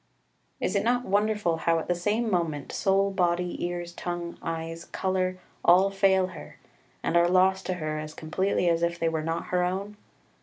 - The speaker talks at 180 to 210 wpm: Yes, average, 190 wpm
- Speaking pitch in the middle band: Yes, medium, 180 Hz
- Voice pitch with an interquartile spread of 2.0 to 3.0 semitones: Yes, narrow, 2.4 semitones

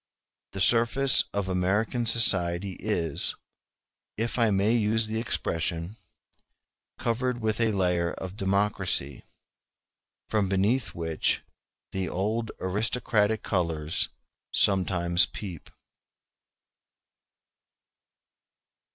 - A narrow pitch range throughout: No, average, 3.7 semitones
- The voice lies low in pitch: Yes, low, 100 Hz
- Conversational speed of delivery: No, slow, 85 wpm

